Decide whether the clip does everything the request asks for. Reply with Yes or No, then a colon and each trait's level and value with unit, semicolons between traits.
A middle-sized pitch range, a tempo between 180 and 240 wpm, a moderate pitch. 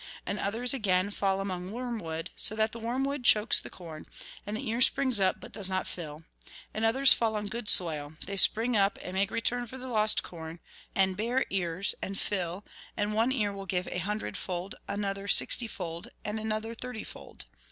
No: average, 3.6 semitones; average, 185 wpm; high, 205 Hz